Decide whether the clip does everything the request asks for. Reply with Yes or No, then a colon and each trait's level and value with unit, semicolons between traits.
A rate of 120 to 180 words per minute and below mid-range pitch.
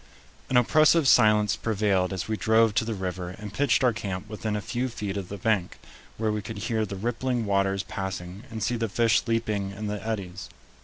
No: fast, 205 wpm; low, 105 Hz